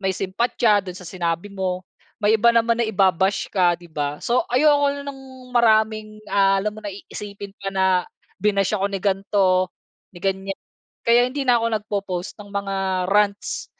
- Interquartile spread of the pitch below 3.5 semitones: Yes, narrow, 2.6 semitones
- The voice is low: No, high, 200 Hz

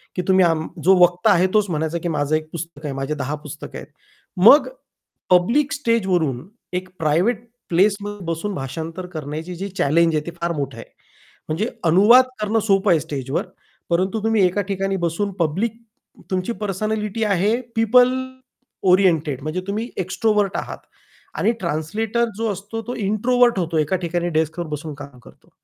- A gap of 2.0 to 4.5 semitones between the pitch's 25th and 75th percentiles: No, average, 4.9 semitones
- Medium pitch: Yes, medium, 180 Hz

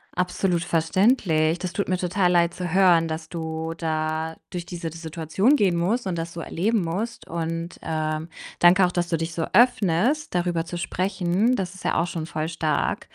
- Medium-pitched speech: Yes, medium, 175 Hz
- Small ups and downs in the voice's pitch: Yes, narrow, 2.3 semitones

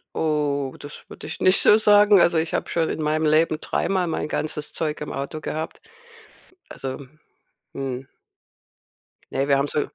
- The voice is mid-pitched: Yes, medium, 155 Hz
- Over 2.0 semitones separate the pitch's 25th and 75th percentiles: Yes, narrow, 2.5 semitones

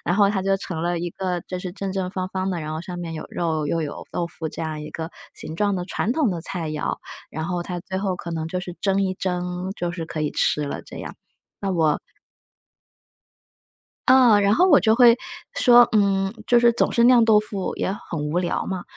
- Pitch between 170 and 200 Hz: Yes, medium, 185 Hz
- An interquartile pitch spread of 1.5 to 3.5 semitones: Yes, average, 3.0 semitones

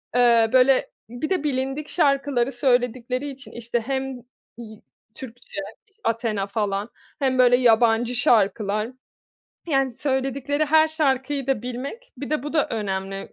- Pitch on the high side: Yes, very high, 255 Hz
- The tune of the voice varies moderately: Yes, average, 3.3 semitones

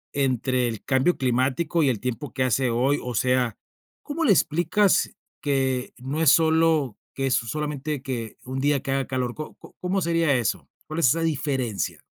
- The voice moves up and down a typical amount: Yes, average, 3.7 semitones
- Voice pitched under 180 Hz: Yes, low, 135 Hz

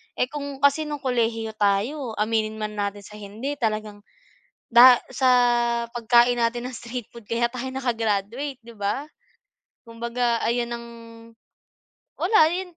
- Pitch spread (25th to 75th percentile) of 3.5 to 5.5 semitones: No, average, 3.0 semitones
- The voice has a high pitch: Yes, high, 235 Hz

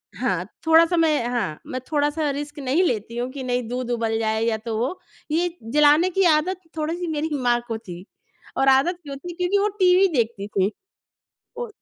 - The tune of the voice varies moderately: No, wide, 6.2 semitones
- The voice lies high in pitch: Yes, very high, 290 Hz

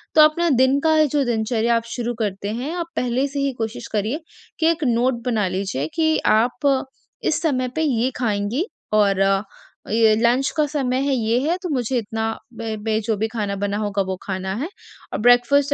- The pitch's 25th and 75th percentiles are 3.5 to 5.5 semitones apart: Yes, average, 4.4 semitones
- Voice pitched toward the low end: No, high, 240 Hz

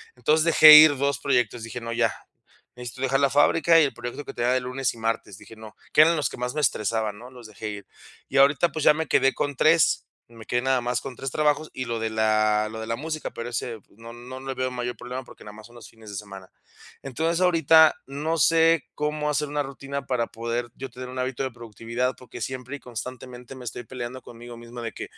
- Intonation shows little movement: No, average, 3.3 semitones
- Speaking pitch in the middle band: No, low, 125 Hz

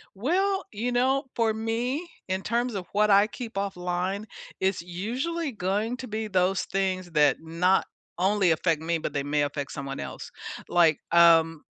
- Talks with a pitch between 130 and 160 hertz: No, high, 195 Hz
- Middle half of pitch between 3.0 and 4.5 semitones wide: No, average, 5.1 semitones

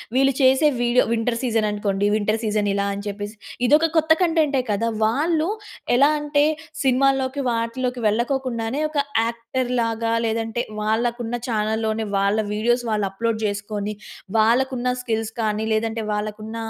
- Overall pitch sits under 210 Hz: No, high, 230 Hz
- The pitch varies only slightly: No, average, 3.2 semitones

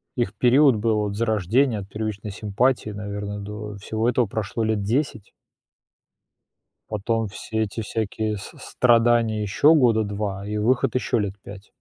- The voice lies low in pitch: Yes, low, 110 Hz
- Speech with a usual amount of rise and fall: No, narrow, 2.2 semitones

